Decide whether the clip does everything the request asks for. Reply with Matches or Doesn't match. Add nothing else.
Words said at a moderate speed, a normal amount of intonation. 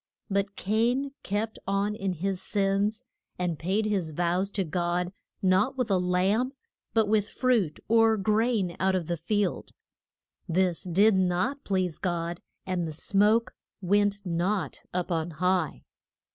Matches